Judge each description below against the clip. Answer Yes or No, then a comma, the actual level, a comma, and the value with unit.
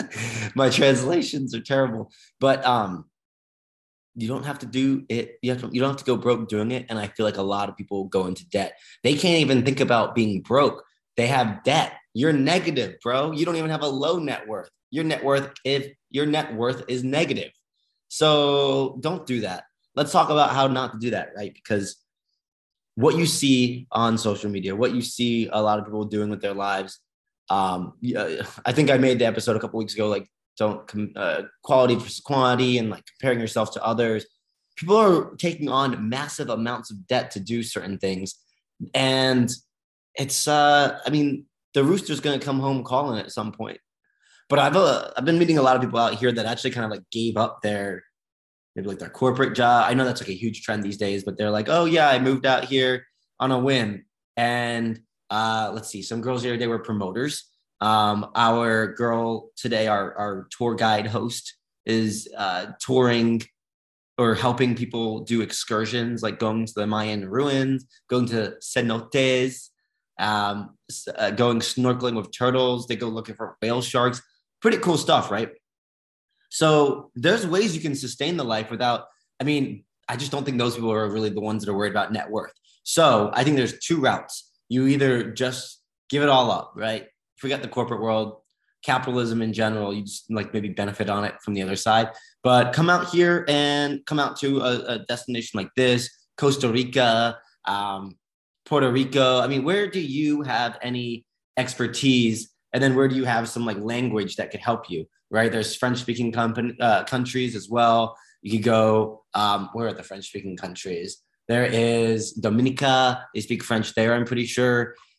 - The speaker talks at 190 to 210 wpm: Yes, average, 195 wpm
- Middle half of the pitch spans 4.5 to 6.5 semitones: No, average, 3.3 semitones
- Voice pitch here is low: Yes, low, 120 Hz